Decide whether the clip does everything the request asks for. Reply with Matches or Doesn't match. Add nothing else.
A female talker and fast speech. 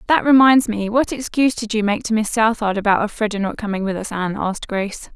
Matches